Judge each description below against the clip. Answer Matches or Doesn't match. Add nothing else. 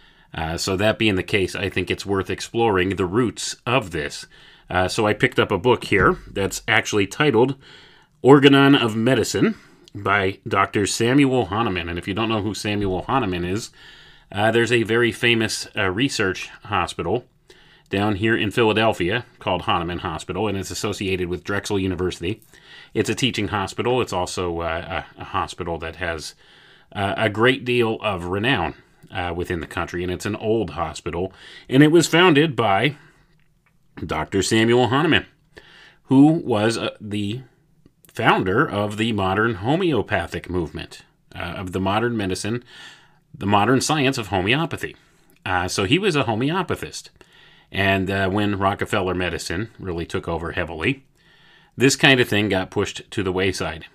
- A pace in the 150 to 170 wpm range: Matches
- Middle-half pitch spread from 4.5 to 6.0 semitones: Matches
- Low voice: Matches